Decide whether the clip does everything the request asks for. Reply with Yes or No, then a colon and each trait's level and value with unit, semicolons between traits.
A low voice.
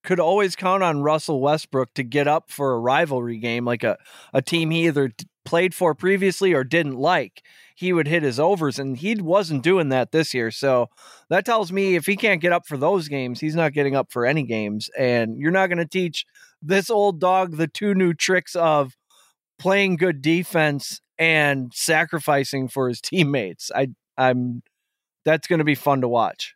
No: medium, 160 Hz